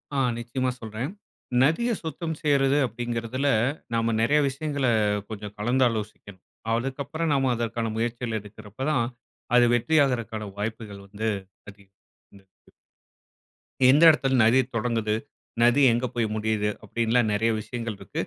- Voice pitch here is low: Yes, low, 115 Hz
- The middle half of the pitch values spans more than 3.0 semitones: Yes, average, 3.4 semitones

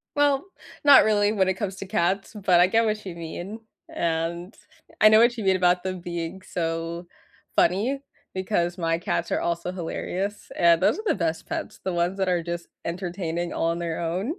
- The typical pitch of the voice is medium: Yes, medium, 180 Hz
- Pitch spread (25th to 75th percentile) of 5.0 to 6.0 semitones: No, average, 2.9 semitones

